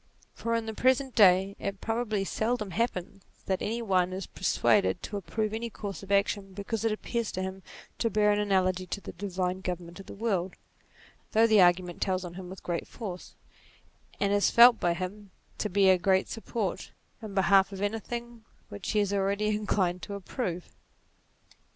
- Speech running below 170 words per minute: No, average, 180 wpm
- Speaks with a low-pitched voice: No, high, 200 Hz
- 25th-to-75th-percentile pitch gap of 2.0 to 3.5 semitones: Yes, average, 2.7 semitones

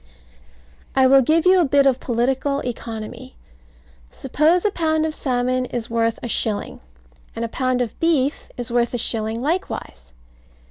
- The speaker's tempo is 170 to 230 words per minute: No, average, 155 wpm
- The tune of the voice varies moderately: Yes, average, 4.3 semitones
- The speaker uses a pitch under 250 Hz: No, very high, 255 Hz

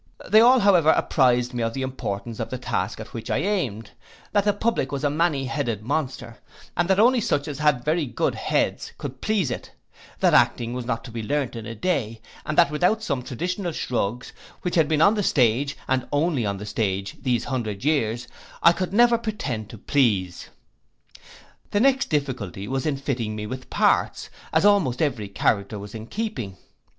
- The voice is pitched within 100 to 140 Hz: Yes, low, 135 Hz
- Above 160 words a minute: Yes, average, 195 wpm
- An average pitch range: No, wide, 7.0 semitones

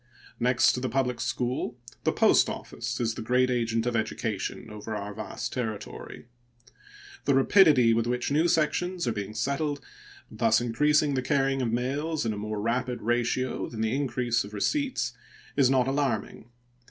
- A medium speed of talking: Yes, average, 165 wpm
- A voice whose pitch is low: Yes, low, 125 Hz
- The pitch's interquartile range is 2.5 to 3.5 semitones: Yes, average, 3.2 semitones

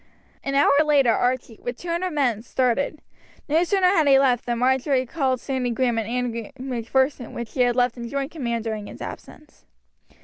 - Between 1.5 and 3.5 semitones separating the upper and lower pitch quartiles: Yes, average, 2.9 semitones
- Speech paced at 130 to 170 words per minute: No, average, 190 wpm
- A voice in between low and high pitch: No, very high, 255 Hz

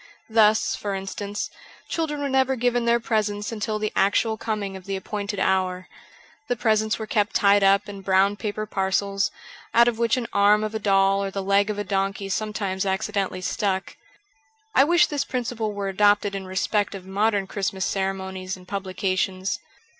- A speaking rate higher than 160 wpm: Yes, average, 175 wpm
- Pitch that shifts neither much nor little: No, narrow, 2.0 semitones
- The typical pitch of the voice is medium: No, high, 205 Hz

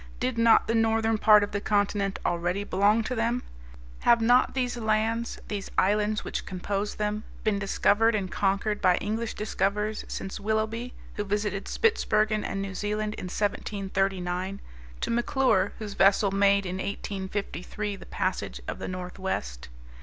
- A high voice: Yes, high, 205 Hz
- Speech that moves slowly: No, average, 150 wpm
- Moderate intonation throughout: No, narrow, 2.0 semitones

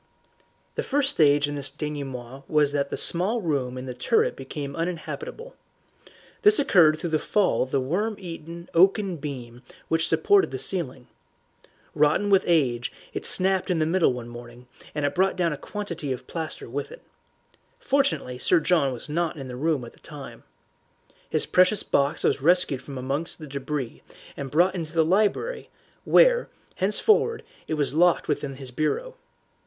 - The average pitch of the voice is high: No, medium, 155 Hz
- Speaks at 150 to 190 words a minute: Yes, average, 170 wpm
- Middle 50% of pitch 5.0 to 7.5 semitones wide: Yes, wide, 5.4 semitones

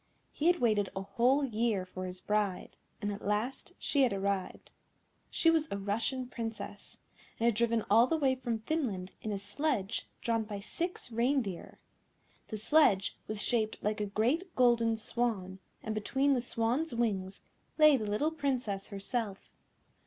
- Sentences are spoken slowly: No, average, 160 wpm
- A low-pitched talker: No, high, 225 Hz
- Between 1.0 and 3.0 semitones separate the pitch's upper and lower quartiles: No, average, 4.3 semitones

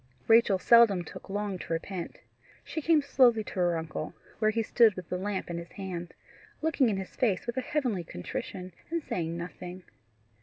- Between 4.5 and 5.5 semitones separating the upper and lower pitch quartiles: Yes, average, 5.0 semitones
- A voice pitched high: Yes, high, 195 Hz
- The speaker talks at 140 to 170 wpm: No, average, 185 wpm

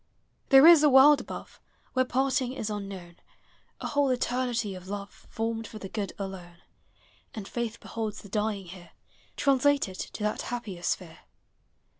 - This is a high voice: Yes, high, 220 Hz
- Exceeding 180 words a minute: No, average, 155 wpm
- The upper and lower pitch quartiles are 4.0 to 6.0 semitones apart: Yes, average, 4.8 semitones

